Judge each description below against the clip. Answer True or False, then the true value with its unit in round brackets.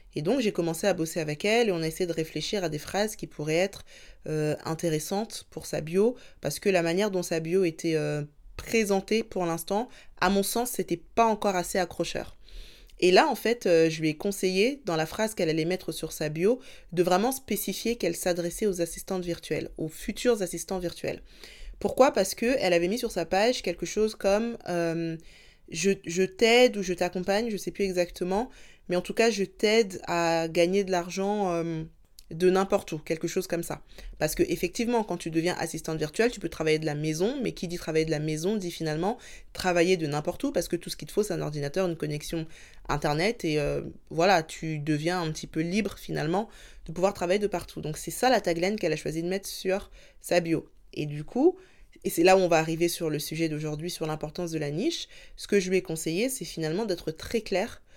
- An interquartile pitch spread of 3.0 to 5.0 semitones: True (3.7 semitones)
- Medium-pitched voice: True (180 Hz)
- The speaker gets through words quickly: True (225 wpm)